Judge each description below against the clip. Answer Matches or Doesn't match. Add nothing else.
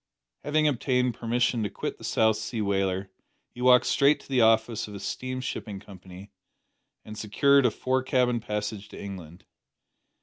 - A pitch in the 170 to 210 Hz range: Doesn't match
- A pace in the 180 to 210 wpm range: Doesn't match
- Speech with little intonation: Doesn't match